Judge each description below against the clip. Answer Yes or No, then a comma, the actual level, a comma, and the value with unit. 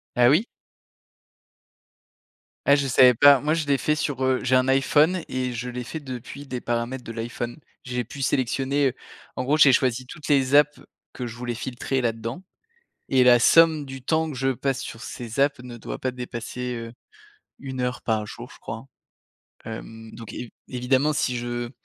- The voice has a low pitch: Yes, low, 130 Hz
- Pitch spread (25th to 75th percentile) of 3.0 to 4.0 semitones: No, narrow, 2.5 semitones